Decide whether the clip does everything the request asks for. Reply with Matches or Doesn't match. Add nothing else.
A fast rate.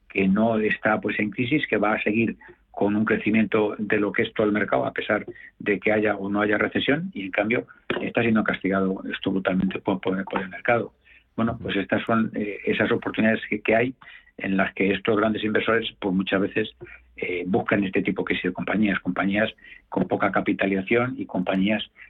Matches